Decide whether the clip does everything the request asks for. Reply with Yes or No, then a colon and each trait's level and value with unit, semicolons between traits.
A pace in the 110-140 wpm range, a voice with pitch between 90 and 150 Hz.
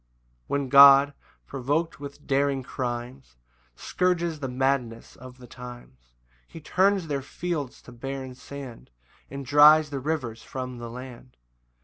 Yes: slow, 135 wpm; low, 135 Hz